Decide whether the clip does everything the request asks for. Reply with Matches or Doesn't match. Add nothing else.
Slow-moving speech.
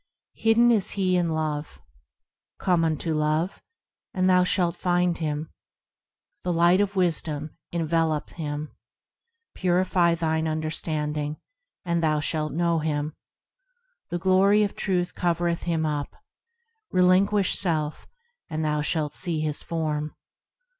Matches